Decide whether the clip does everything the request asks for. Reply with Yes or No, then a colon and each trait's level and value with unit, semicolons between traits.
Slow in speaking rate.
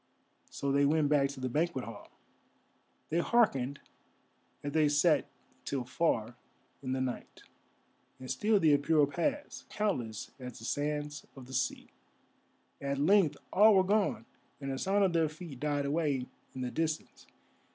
No: average, 155 wpm